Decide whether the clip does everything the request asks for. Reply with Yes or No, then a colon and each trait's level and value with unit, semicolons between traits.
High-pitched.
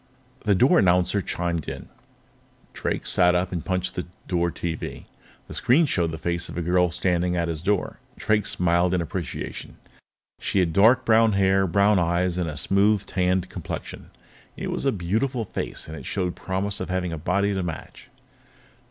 No: very low, 90 Hz